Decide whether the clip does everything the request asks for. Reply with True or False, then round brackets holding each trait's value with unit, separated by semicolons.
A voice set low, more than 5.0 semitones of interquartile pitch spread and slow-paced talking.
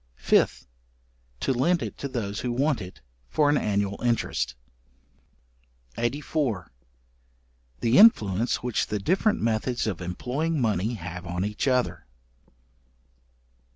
True (120 Hz; 5.6 semitones; 120 wpm)